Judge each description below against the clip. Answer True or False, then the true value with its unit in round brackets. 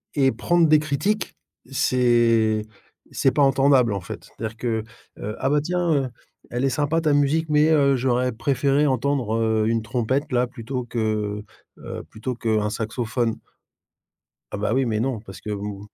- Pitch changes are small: False (4.2 semitones)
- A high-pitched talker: False (125 Hz)